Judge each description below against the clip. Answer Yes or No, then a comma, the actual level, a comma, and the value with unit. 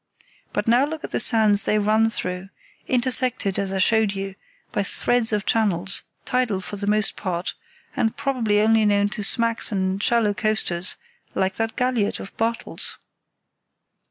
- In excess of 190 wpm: No, average, 155 wpm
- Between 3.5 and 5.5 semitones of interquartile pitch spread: No, average, 2.8 semitones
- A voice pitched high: Yes, high, 215 Hz